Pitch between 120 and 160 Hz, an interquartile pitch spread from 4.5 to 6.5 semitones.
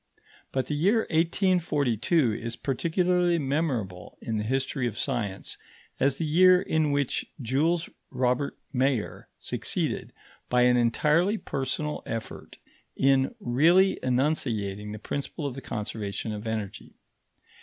Yes: low, 135 Hz; wide, 5.5 semitones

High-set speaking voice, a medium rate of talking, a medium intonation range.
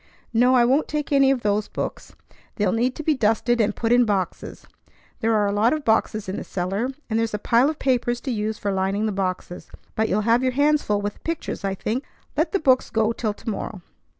No: high, 225 Hz; fast, 235 wpm; average, 3.7 semitones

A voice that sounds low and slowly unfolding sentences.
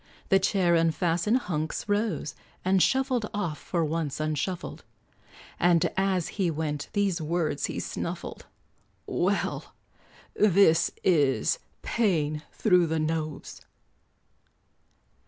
No: medium, 170 Hz; slow, 100 wpm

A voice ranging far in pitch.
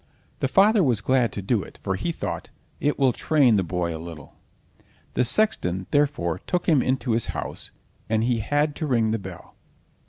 Yes: wide, 7.3 semitones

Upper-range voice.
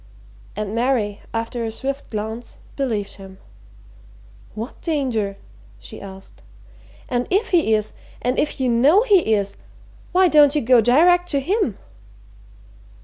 Yes: high, 245 Hz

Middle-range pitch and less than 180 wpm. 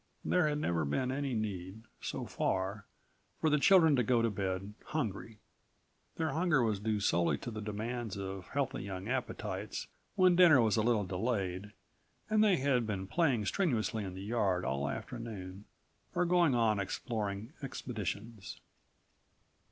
No: low, 110 Hz; average, 150 wpm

